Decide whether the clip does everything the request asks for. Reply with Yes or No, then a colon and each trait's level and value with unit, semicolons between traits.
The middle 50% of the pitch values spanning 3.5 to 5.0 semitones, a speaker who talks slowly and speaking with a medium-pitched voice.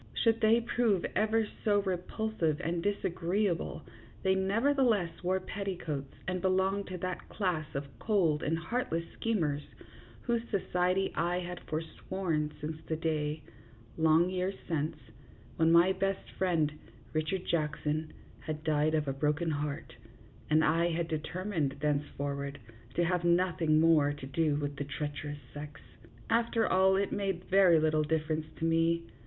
No: average, 3.8 semitones; average, 145 wpm; medium, 165 Hz